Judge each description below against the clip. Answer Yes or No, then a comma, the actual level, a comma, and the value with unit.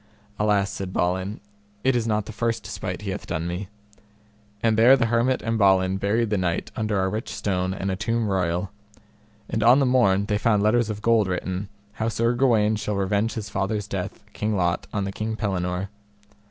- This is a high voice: No, low, 105 Hz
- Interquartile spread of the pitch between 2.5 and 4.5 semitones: Yes, average, 2.9 semitones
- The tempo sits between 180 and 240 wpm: Yes, average, 195 wpm